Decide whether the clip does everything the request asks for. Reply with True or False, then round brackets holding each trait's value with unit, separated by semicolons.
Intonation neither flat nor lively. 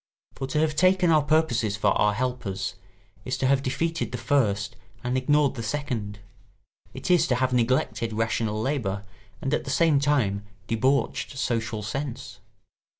True (4.7 semitones)